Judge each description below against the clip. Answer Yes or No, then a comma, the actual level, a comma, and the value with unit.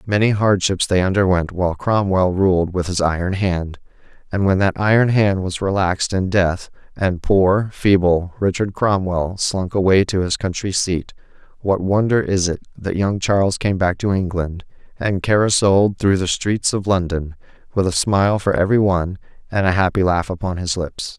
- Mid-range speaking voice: No, very low, 95 Hz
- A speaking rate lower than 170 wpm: No, average, 175 wpm